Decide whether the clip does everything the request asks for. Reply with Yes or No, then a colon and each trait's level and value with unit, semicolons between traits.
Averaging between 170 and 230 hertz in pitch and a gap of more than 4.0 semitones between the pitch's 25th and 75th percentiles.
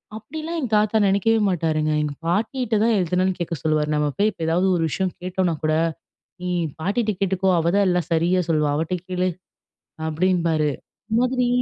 Yes: medium, 185 Hz; average, 4.4 semitones